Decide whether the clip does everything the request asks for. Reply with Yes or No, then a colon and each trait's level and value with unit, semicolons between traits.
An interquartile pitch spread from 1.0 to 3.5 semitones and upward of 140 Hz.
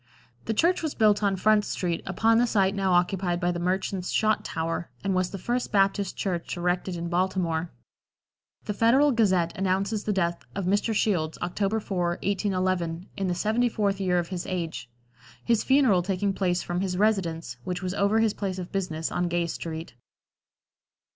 Yes: average, 2.8 semitones; high, 190 Hz